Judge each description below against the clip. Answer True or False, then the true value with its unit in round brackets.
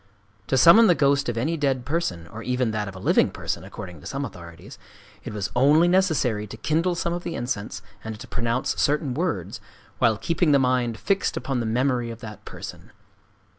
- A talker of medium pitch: False (125 Hz)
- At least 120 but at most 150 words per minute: False (190 wpm)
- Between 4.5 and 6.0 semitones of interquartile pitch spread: True (5.6 semitones)